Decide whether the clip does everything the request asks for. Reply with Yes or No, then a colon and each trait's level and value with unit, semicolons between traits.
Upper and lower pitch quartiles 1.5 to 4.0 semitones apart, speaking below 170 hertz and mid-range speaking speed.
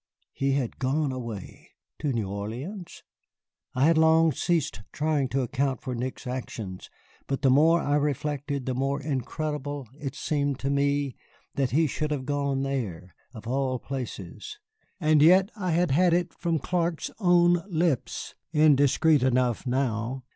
Yes: average, 3.4 semitones; medium, 140 Hz; average, 150 wpm